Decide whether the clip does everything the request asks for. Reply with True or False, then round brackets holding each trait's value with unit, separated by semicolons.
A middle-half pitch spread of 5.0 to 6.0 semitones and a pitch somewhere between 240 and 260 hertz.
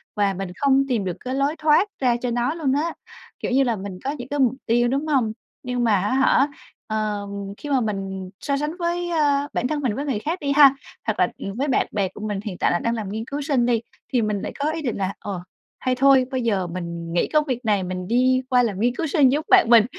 True (5.3 semitones; 245 Hz)